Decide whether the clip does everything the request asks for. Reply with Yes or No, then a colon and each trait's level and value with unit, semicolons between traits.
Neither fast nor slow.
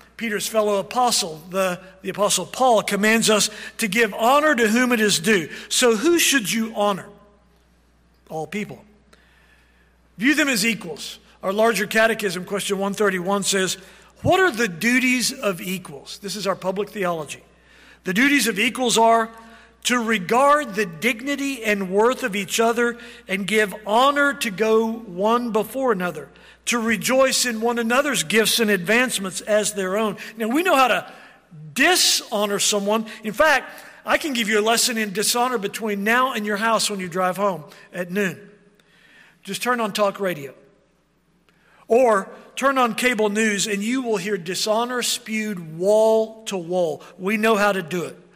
Yes: average, 165 wpm